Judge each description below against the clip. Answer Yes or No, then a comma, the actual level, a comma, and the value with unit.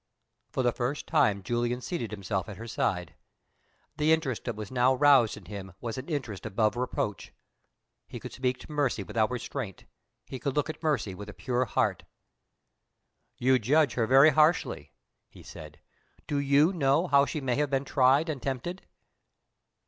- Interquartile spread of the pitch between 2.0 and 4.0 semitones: No, average, 4.5 semitones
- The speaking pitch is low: Yes, low, 130 Hz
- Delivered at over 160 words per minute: Yes, average, 170 wpm